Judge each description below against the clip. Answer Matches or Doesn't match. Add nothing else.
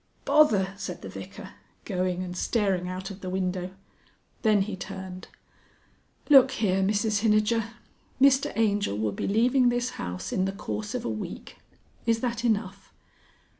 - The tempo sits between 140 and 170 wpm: Matches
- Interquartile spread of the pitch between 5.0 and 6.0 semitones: Doesn't match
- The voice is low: Doesn't match